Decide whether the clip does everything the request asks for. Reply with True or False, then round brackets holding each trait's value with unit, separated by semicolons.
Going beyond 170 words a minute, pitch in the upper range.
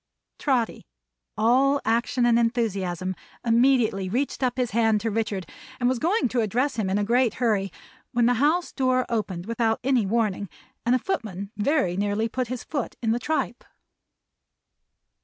False (160 wpm; 230 Hz)